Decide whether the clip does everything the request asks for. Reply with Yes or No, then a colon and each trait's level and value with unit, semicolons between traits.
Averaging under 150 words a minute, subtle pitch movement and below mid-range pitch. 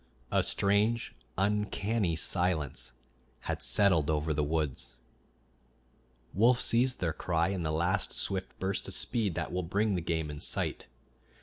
No: average, 140 wpm; average, 4.2 semitones; very low, 90 Hz